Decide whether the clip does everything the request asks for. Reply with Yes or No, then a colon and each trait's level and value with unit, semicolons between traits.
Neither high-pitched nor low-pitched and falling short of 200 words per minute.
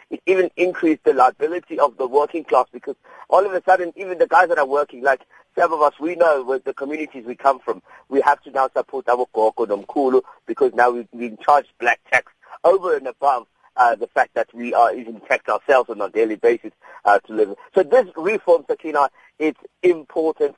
No: medium, 165 Hz; fast, 205 wpm